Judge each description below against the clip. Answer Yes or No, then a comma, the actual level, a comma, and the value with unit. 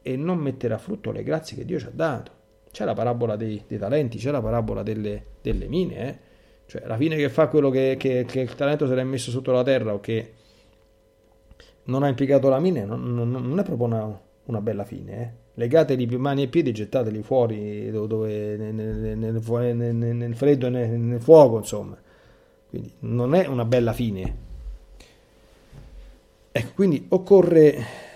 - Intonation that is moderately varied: Yes, average, 3.7 semitones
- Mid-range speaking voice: No, low, 120 Hz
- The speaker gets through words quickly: Yes, fast, 185 wpm